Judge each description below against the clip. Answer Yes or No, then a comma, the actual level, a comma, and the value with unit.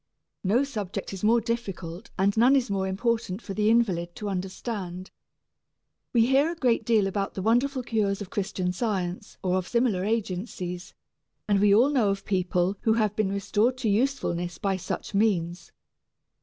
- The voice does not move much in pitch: No, average, 3.7 semitones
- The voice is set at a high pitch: Yes, high, 205 Hz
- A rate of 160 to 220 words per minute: Yes, average, 170 wpm